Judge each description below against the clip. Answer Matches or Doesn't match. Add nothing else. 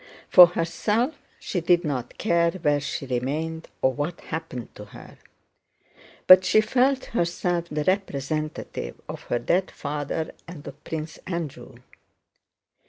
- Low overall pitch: Doesn't match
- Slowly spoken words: Matches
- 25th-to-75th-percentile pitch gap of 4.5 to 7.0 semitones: Doesn't match